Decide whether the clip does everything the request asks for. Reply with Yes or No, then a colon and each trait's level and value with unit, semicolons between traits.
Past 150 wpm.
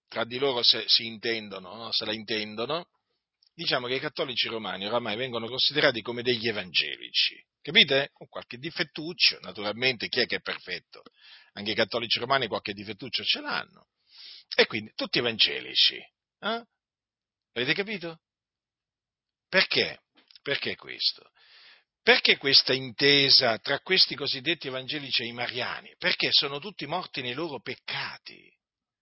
No: average, 135 wpm